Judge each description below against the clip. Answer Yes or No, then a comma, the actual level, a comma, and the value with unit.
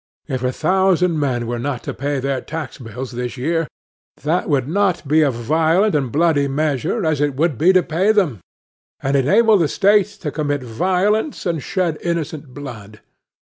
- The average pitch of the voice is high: No, medium, 150 Hz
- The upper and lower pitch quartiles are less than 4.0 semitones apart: No, average, 4.9 semitones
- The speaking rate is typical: Yes, average, 175 wpm